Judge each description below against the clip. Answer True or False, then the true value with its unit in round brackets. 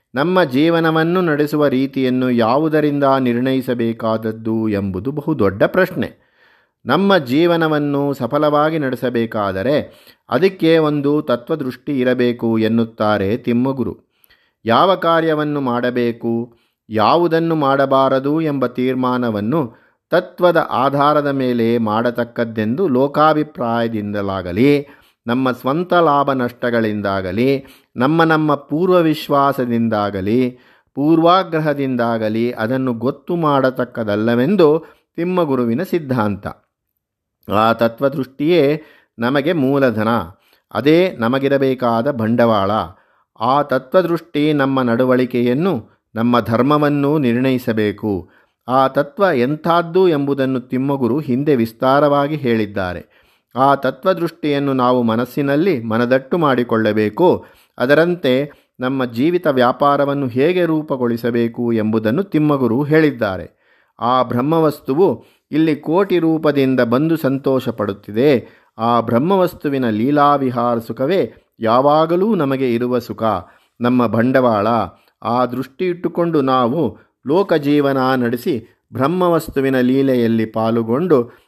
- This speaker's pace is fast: False (80 wpm)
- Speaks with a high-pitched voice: False (130 Hz)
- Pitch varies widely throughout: False (4.1 semitones)